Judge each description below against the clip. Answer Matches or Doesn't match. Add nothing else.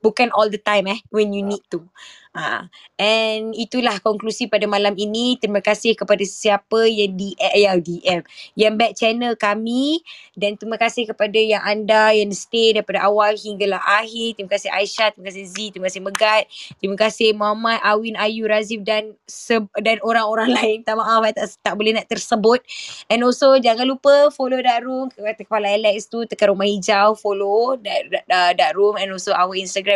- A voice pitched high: Matches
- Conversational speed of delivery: Doesn't match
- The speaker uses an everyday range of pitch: Doesn't match